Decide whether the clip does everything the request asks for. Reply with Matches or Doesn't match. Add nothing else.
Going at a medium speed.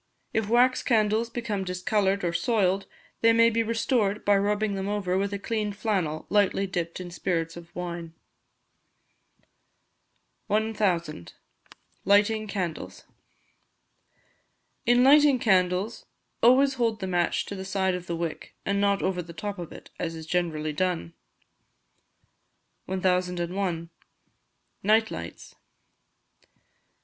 Doesn't match